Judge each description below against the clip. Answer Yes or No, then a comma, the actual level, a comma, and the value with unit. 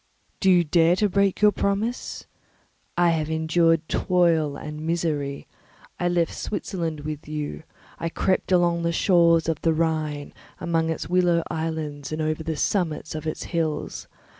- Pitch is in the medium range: Yes, medium, 165 Hz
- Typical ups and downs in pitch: No, narrow, 2.1 semitones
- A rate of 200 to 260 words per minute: No, average, 155 wpm